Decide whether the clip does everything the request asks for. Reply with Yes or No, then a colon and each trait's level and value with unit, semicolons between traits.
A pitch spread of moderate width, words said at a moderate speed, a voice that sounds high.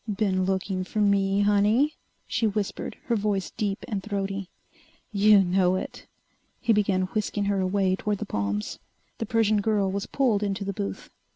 No: narrow, 1.8 semitones; average, 165 wpm; high, 200 Hz